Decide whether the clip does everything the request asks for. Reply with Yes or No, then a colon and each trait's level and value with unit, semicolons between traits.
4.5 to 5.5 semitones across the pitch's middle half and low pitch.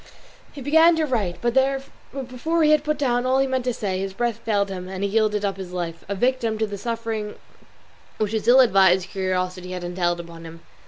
No: average, 5.2 semitones; high, 210 Hz